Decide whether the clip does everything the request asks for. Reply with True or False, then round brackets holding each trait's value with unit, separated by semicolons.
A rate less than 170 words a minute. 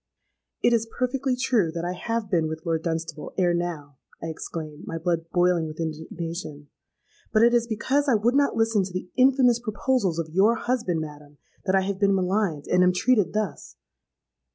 False (185 wpm)